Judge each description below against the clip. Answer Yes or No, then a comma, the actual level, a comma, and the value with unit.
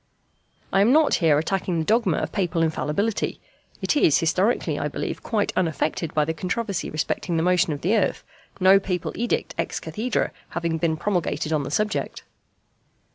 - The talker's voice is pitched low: No, medium, 180 Hz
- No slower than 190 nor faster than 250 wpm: No, average, 170 wpm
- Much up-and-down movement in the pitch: No, average, 4.4 semitones